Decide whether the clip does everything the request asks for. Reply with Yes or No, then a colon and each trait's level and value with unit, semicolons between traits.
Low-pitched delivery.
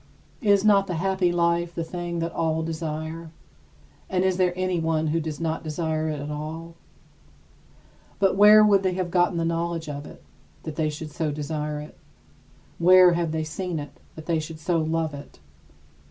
No: medium, 165 Hz